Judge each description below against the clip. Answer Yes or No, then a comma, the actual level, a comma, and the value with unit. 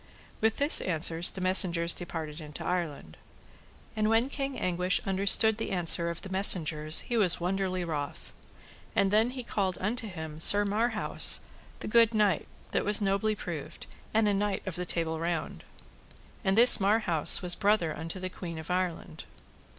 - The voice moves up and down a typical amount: Yes, average, 4.0 semitones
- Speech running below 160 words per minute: No, average, 165 wpm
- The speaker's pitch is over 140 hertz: Yes, medium, 185 Hz